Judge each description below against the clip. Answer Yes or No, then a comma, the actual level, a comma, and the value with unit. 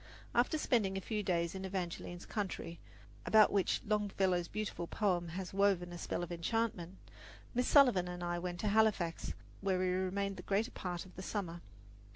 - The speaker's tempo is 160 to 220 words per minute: Yes, average, 175 wpm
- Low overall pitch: No, high, 190 Hz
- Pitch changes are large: No, average, 2.9 semitones